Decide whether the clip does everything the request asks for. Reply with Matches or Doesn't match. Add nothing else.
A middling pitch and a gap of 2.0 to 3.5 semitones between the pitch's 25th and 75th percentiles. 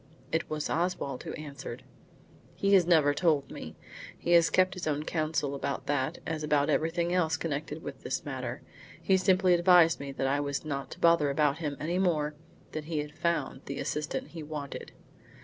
Matches